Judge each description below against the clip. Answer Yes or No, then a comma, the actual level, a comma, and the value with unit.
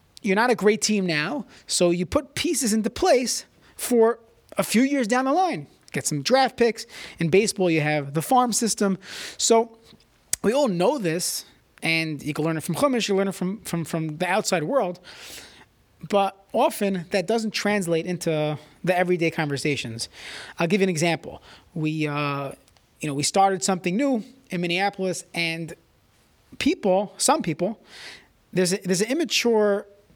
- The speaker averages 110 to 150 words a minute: No, average, 165 wpm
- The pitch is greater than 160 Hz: Yes, high, 190 Hz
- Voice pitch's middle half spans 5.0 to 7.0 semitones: Yes, wide, 5.4 semitones